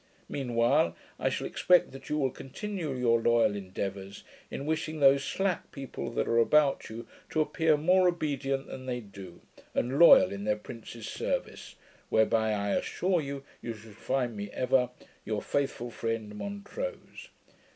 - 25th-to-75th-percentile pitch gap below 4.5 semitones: No, wide, 5.4 semitones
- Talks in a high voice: No, low, 130 Hz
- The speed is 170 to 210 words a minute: No, average, 160 wpm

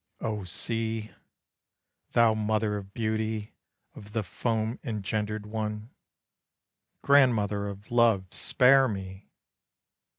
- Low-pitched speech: Yes, low, 110 Hz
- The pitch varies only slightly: Yes, narrow, 1.6 semitones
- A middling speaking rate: No, slow, 95 wpm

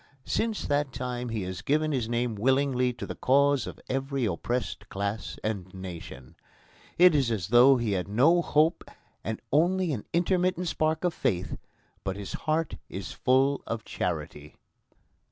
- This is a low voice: Yes, low, 125 Hz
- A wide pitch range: Yes, wide, 6.7 semitones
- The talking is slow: No, average, 155 wpm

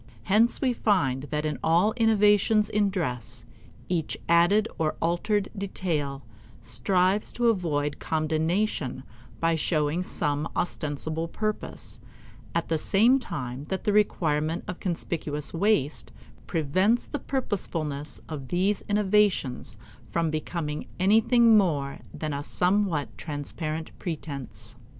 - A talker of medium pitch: Yes, medium, 170 Hz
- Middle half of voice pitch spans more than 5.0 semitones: Yes, wide, 5.5 semitones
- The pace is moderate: No, slow, 115 wpm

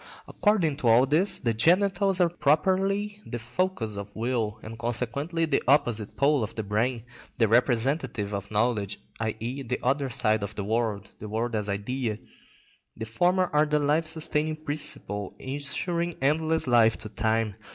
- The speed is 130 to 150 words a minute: No, average, 160 wpm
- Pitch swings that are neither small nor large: No, wide, 5.9 semitones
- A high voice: No, low, 125 Hz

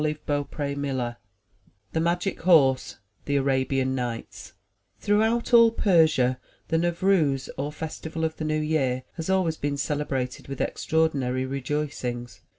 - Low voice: No, medium, 150 Hz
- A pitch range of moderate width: Yes, average, 3.5 semitones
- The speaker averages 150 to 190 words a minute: No, slow, 135 wpm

